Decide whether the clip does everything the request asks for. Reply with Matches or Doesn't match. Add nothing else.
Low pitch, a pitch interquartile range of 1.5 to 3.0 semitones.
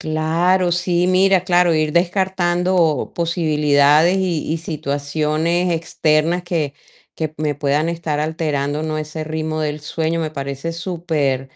Doesn't match